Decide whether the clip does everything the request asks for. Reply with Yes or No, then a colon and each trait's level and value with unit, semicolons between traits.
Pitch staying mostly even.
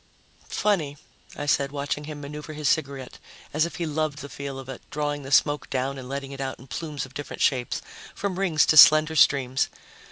Yes: narrow, 2.1 semitones